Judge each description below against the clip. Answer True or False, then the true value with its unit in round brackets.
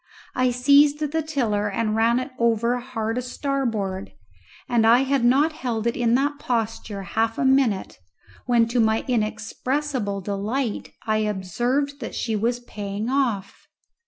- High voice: True (235 Hz)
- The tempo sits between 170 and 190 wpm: False (150 wpm)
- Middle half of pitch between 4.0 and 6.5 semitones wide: False (3.5 semitones)